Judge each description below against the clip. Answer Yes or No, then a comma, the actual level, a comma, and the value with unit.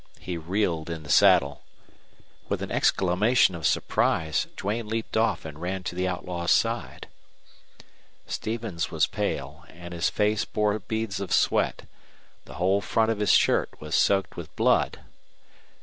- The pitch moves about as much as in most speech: Yes, average, 3.9 semitones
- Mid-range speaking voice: No, very low, 95 Hz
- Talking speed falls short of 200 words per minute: Yes, average, 150 wpm